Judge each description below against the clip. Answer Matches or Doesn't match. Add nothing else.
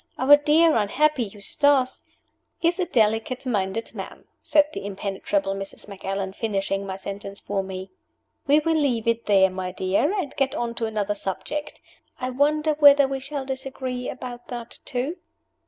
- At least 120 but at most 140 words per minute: Doesn't match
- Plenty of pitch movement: Matches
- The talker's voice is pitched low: Doesn't match